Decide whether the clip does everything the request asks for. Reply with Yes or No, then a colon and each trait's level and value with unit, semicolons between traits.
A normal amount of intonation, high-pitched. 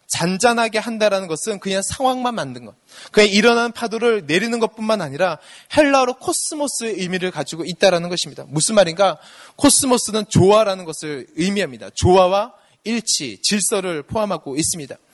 Yes: average, 4.5 semitones; high, 205 Hz